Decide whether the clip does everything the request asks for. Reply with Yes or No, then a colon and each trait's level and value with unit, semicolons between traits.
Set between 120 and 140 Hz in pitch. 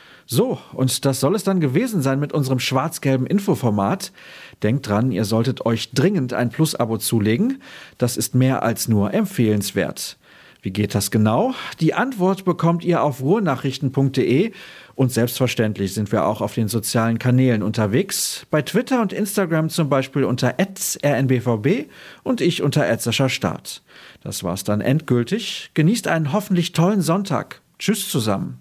Yes: low, 135 Hz